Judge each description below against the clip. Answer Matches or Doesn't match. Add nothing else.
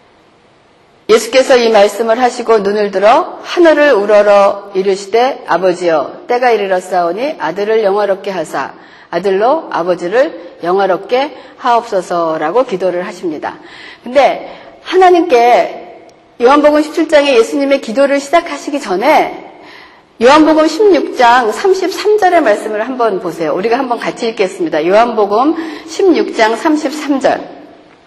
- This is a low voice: Doesn't match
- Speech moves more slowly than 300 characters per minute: Matches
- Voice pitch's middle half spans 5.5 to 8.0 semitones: Doesn't match